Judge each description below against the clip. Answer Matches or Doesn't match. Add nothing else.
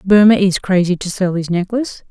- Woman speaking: Matches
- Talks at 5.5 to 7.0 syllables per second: Matches